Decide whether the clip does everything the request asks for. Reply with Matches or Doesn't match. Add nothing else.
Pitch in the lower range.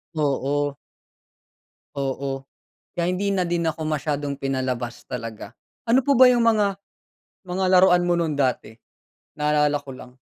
Doesn't match